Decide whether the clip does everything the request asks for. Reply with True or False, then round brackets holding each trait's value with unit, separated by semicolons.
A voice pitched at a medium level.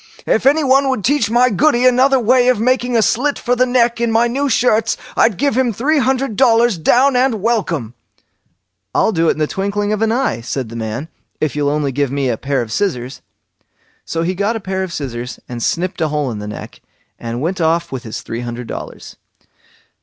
False (205 Hz)